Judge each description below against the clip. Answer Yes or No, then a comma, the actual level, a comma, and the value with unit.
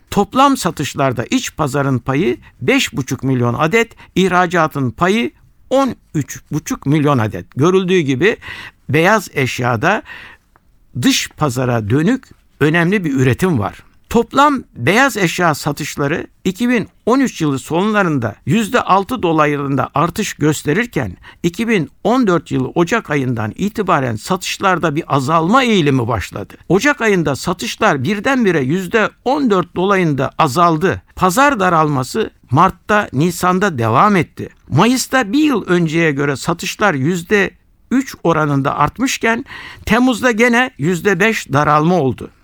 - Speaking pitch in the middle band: Yes, medium, 175 Hz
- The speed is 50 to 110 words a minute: Yes, average, 100 wpm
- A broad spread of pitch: Yes, wide, 7.2 semitones